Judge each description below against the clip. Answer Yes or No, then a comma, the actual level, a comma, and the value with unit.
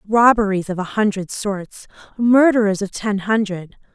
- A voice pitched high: Yes, high, 205 Hz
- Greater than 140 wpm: No, slow, 135 wpm